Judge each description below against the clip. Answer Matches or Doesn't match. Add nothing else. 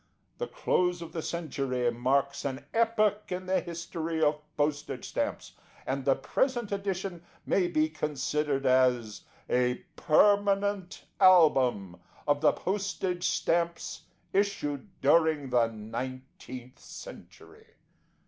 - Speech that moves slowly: Matches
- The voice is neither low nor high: Matches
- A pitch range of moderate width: Doesn't match